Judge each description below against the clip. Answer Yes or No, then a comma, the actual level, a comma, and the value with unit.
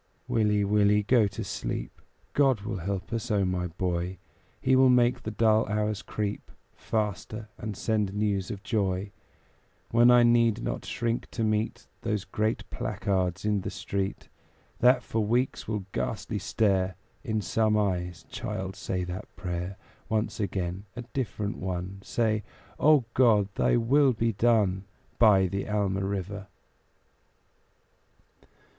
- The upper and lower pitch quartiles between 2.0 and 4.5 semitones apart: Yes, average, 3.0 semitones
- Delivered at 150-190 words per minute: No, average, 140 wpm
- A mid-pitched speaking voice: No, low, 105 Hz